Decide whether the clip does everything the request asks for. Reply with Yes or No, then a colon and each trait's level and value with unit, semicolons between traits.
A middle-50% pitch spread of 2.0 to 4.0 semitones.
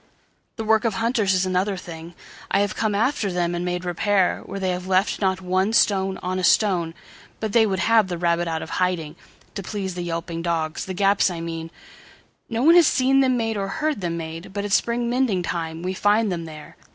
Yes: average, 3.6 semitones